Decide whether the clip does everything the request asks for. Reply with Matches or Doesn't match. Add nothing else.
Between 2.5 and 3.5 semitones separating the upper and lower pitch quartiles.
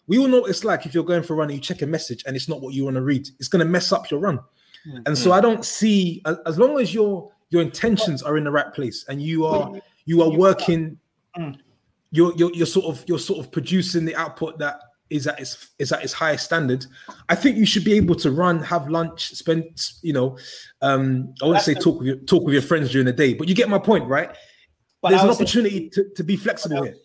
Doesn't match